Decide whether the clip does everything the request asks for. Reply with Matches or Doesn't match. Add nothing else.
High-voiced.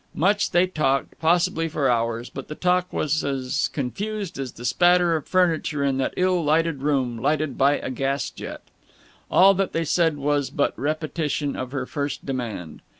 Doesn't match